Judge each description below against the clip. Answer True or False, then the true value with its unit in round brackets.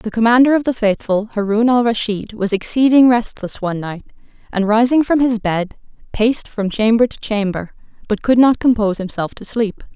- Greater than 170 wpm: True (180 wpm)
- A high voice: True (220 Hz)